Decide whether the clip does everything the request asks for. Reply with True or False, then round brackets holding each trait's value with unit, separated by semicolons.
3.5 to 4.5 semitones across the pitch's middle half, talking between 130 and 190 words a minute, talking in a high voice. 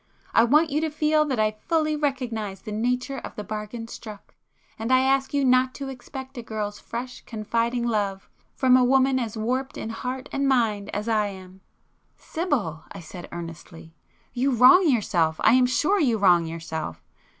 True (4.2 semitones; 170 wpm; 240 Hz)